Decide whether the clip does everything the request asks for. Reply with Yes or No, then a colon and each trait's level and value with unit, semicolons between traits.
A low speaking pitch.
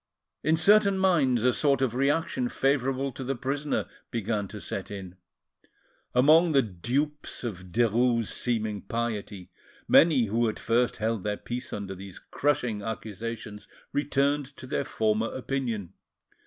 Yes: low, 120 Hz